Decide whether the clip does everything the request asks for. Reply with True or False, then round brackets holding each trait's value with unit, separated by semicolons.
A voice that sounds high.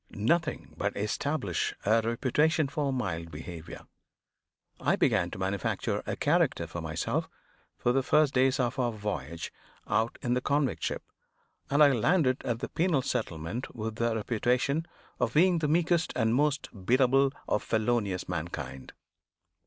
False (125 Hz)